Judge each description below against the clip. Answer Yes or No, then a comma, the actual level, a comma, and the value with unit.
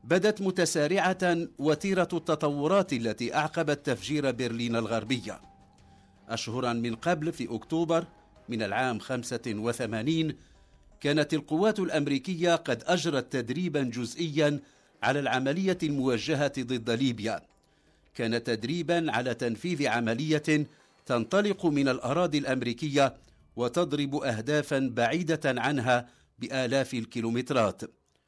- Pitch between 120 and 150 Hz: Yes, low, 135 Hz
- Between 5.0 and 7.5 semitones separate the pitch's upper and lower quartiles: Yes, average, 5.3 semitones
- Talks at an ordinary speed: No, slow, 95 wpm